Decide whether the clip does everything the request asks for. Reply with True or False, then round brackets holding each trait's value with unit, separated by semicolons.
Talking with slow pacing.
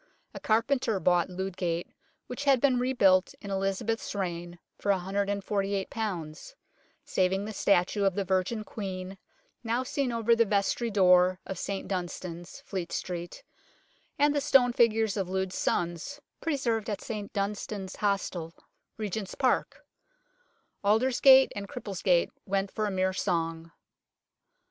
True (130 wpm)